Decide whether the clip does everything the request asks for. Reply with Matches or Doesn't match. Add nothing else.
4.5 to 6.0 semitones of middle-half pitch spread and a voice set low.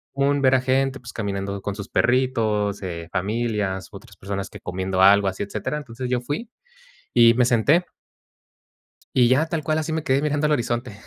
Matches